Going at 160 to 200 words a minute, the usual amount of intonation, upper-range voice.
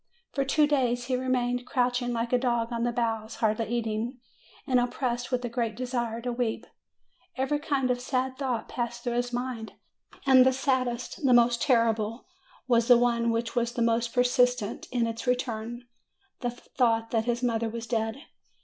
No: average, 180 wpm; narrow, 1.4 semitones; high, 240 Hz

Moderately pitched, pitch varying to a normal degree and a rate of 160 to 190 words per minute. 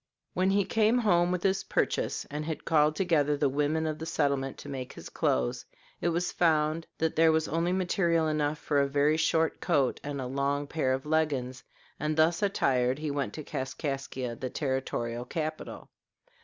Yes: medium, 155 Hz; average, 3.1 semitones; average, 185 wpm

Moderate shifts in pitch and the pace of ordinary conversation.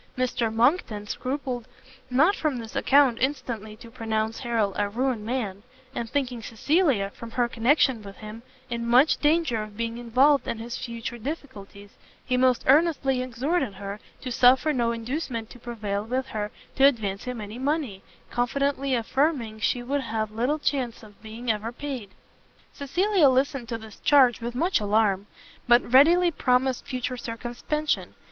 Yes: average, 3.5 semitones; average, 155 wpm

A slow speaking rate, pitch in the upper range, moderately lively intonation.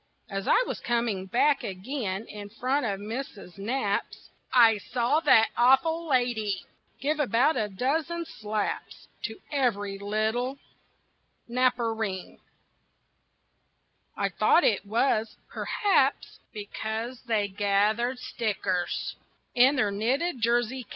Yes: slow, 110 wpm; high, 230 Hz; average, 4.0 semitones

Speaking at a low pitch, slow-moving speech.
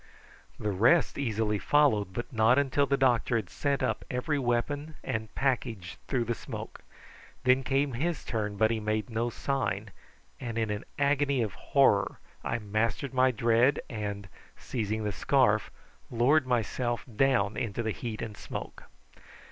No: low, 120 Hz; average, 155 wpm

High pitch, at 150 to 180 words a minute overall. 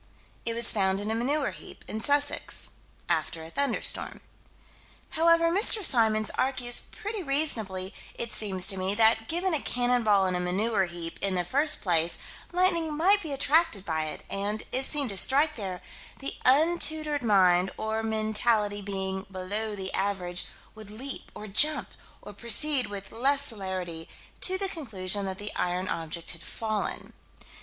Yes: high, 220 Hz; average, 160 wpm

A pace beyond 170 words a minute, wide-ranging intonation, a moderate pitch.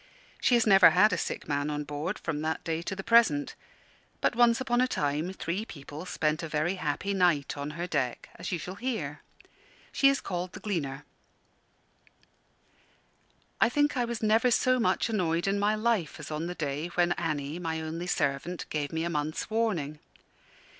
Yes: average, 185 wpm; wide, 6.0 semitones; medium, 175 Hz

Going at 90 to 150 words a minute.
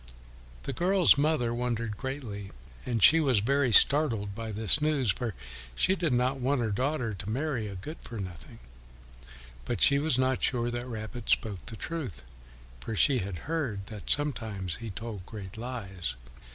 No: average, 165 wpm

